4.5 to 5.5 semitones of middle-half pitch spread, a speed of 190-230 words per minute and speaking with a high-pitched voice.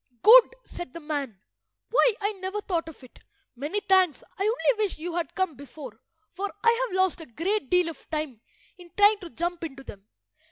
Yes: average, 5.2 semitones; average, 195 wpm; very high, 350 Hz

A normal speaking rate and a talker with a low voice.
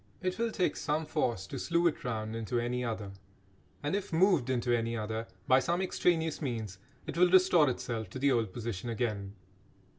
Yes: average, 185 wpm; low, 125 Hz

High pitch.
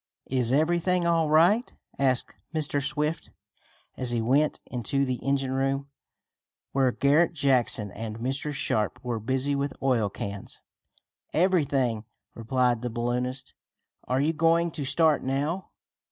No: low, 135 Hz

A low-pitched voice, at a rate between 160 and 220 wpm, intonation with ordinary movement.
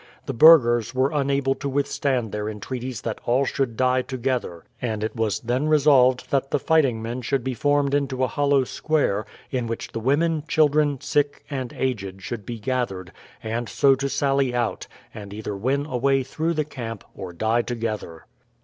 Yes: low, 130 Hz; average, 180 wpm; average, 3.5 semitones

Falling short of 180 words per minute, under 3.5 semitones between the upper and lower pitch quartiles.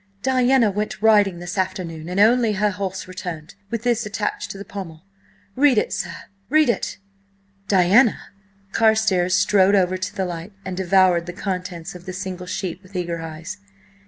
Yes: average, 160 wpm; average, 2.8 semitones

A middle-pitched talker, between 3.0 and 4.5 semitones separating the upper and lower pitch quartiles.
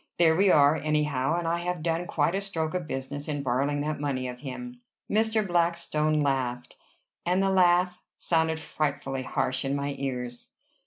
Yes: medium, 155 Hz; average, 4.0 semitones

